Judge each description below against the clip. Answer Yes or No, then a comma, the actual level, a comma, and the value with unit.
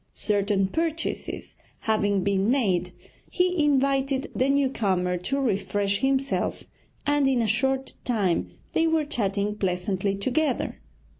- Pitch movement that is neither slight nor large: No, wide, 5.8 semitones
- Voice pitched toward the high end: Yes, high, 230 Hz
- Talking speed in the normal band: No, slow, 125 wpm